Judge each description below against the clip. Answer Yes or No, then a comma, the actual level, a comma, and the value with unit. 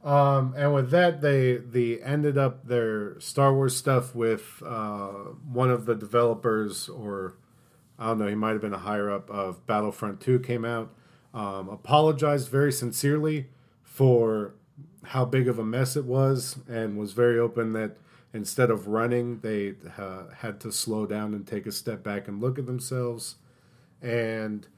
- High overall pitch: No, low, 120 Hz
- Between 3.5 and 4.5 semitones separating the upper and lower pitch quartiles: Yes, average, 3.9 semitones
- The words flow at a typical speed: Yes, average, 170 wpm